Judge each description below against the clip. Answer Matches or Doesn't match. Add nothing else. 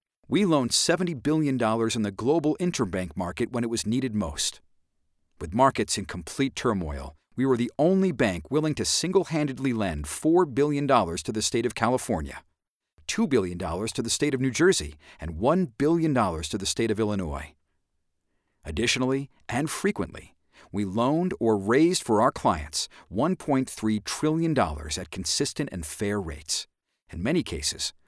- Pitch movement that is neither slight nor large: Doesn't match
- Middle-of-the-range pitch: Doesn't match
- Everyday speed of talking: Matches